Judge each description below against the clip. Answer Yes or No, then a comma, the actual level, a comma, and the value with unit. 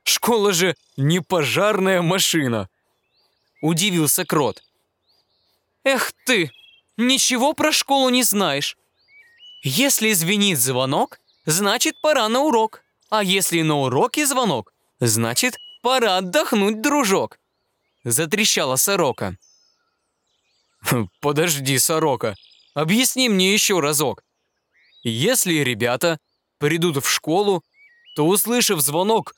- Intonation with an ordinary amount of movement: No, wide, 8.1 semitones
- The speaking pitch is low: No, high, 190 Hz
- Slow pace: Yes, slow, 95 wpm